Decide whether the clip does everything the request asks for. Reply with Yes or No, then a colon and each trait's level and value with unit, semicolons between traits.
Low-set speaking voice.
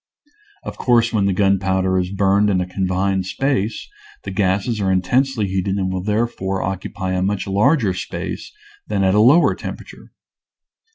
Yes: very low, 95 Hz